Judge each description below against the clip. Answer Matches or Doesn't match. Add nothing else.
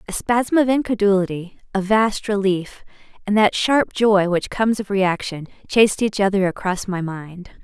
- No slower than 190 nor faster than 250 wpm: Doesn't match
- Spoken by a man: Doesn't match